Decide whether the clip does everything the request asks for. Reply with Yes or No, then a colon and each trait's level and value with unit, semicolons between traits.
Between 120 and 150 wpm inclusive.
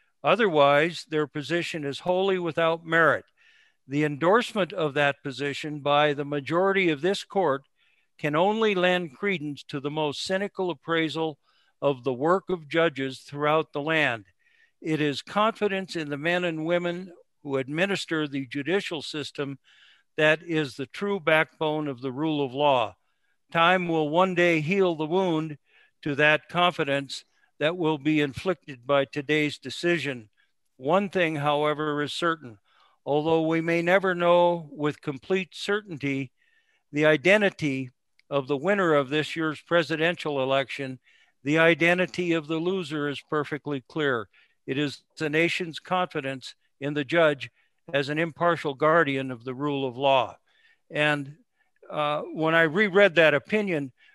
Yes: average, 145 wpm